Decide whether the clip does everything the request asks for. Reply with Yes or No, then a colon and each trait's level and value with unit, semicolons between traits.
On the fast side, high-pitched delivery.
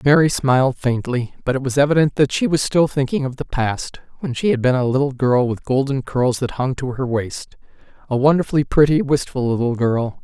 No: fast, 210 wpm; low, 135 Hz